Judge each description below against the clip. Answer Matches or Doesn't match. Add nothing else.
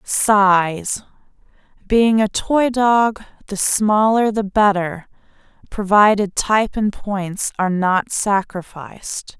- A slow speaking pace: Matches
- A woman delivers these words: Matches